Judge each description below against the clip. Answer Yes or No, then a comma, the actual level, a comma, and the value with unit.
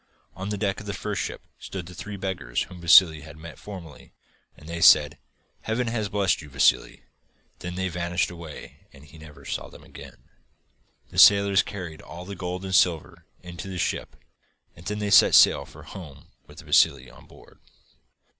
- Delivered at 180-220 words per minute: Yes, average, 185 wpm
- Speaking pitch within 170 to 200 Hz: No, very low, 90 Hz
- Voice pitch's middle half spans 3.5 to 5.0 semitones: Yes, average, 3.8 semitones